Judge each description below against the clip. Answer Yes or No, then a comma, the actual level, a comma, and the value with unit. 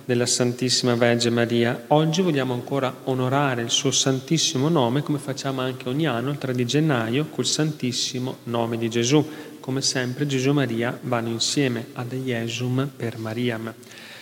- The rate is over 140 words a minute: Yes, average, 155 wpm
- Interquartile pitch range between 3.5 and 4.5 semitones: No, average, 2.8 semitones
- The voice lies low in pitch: Yes, low, 130 Hz